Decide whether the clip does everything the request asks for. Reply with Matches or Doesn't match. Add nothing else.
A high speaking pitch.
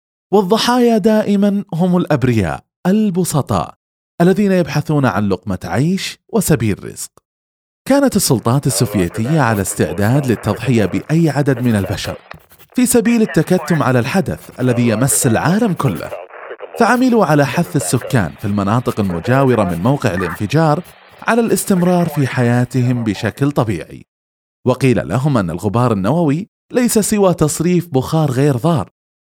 Doesn't match